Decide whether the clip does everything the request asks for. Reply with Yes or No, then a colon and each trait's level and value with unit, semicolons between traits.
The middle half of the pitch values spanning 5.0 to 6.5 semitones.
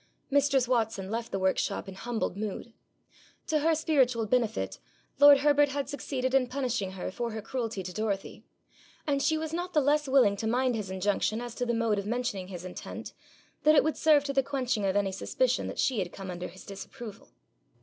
Yes: wide, 5.6 semitones